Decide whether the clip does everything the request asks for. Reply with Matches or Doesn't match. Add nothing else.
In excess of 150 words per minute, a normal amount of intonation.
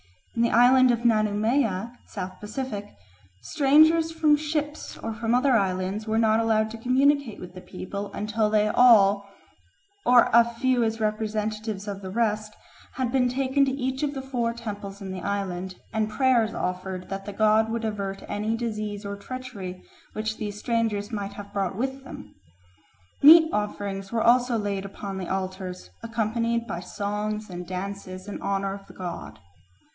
Matches